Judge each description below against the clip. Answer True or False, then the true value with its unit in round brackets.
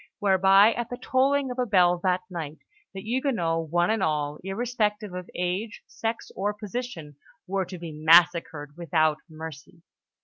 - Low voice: False (185 Hz)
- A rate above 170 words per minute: False (150 wpm)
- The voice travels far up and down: False (4.8 semitones)